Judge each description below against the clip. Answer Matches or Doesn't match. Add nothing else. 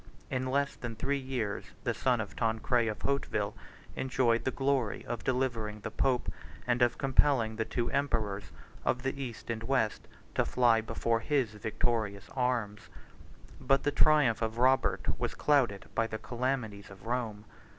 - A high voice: Doesn't match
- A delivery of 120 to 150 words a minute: Doesn't match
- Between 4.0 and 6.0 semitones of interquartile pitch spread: Doesn't match